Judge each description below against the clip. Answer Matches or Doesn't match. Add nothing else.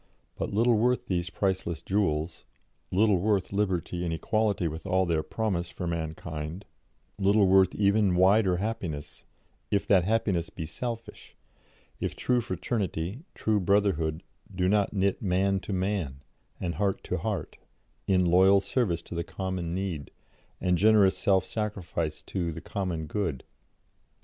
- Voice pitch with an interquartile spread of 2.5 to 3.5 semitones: Matches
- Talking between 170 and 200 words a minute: Doesn't match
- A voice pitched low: Matches